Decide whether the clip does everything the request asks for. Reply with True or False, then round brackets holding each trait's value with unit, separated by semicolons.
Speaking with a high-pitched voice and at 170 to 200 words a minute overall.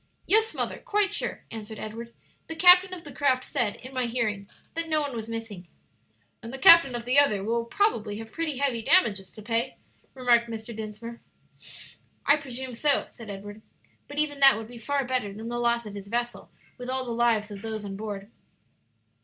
True (235 Hz; 195 wpm)